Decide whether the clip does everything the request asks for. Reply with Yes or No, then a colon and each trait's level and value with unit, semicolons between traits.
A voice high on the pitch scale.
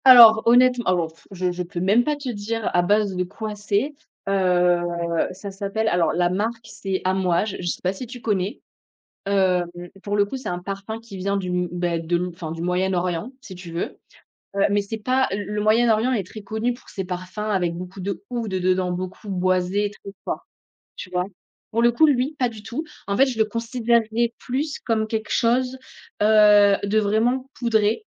Yes: high, 205 Hz